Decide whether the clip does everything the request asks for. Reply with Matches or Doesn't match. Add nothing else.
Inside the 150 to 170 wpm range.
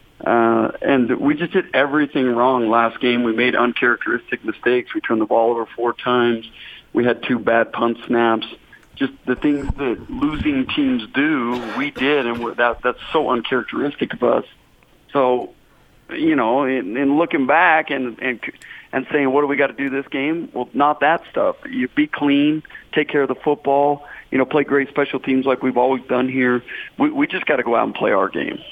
Doesn't match